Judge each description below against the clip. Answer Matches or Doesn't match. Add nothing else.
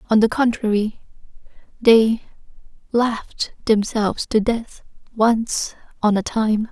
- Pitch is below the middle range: Doesn't match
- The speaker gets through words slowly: Matches